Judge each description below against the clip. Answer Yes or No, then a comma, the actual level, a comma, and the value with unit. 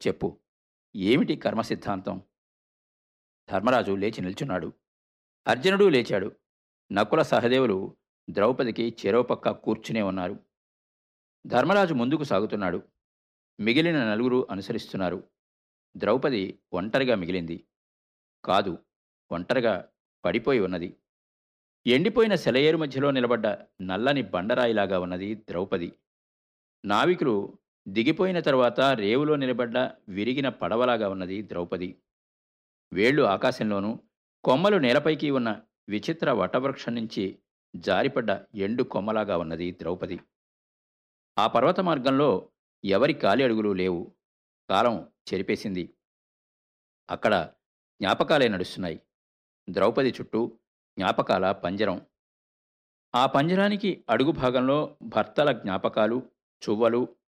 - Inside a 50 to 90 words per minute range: Yes, average, 85 wpm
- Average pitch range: No, wide, 6.4 semitones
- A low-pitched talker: Yes, low, 105 Hz